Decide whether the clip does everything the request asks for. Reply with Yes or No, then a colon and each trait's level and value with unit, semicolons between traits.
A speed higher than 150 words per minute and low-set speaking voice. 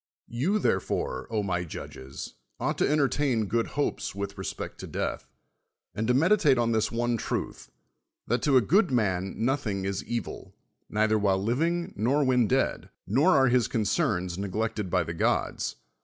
Yes: average, 160 wpm; low, 115 Hz